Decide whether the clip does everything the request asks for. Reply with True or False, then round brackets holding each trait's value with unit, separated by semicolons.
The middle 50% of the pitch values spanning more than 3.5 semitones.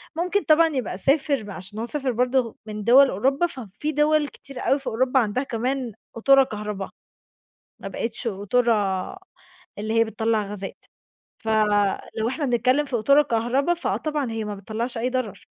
True (4.2 semitones)